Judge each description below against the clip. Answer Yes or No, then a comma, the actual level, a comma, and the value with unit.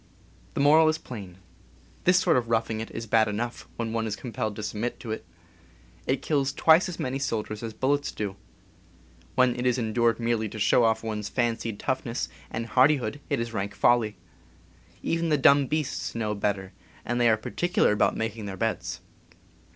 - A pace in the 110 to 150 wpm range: No, average, 185 wpm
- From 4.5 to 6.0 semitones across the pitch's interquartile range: No, average, 3.3 semitones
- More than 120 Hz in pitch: No, low, 115 Hz